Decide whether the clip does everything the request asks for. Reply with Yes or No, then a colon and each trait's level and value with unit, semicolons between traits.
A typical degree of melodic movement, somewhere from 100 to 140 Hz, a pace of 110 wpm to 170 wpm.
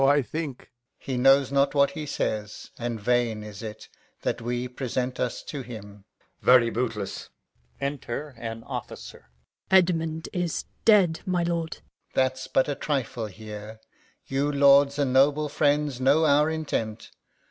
Yes: average, 4.0 semitones; low, 135 Hz; average, 165 wpm